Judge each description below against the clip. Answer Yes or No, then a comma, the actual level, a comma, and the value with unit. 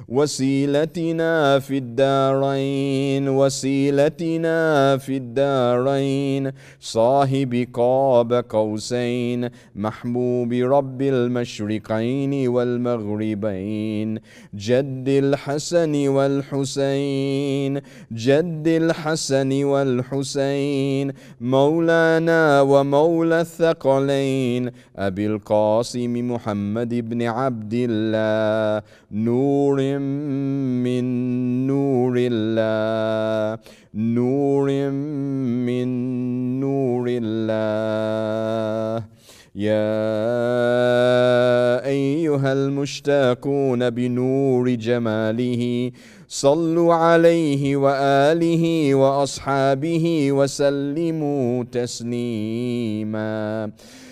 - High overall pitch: No, low, 130 Hz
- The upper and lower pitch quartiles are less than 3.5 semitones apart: Yes, narrow, 2.5 semitones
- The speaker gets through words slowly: Yes, slow, 50 wpm